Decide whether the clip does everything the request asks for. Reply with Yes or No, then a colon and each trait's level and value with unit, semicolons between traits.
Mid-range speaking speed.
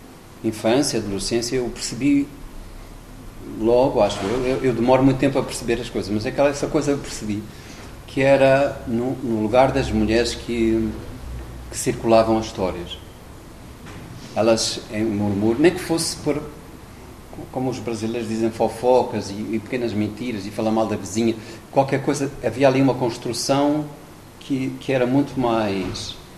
Yes: average, 150 wpm